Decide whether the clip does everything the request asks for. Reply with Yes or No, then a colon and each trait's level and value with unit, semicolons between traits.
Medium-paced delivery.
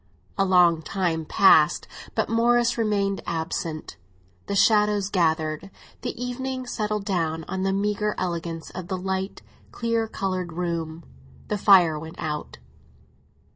No: slow, 130 wpm